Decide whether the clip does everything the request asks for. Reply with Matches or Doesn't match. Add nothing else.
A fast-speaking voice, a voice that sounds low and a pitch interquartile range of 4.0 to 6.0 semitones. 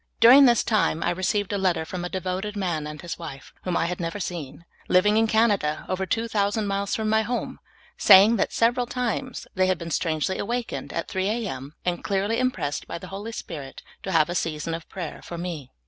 Doesn't match